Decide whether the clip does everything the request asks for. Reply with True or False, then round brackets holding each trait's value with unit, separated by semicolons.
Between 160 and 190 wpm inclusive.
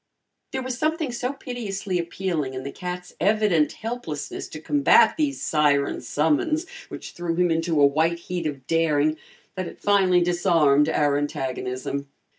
False (150 wpm)